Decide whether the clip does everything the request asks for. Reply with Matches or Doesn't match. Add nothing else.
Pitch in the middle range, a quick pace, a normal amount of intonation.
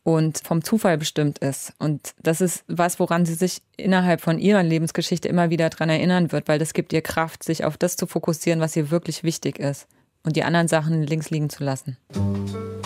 Doesn't match